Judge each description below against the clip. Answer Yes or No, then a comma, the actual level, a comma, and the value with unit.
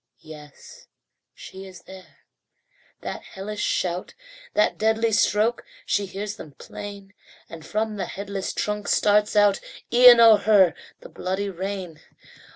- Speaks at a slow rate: Yes, slow, 130 wpm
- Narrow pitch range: Yes, narrow, 2.0 semitones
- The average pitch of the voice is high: Yes, high, 200 Hz